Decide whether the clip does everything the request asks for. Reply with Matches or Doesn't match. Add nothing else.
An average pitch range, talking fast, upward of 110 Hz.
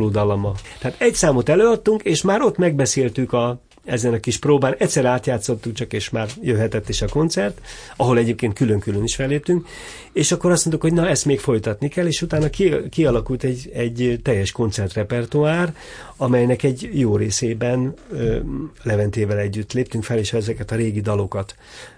Matches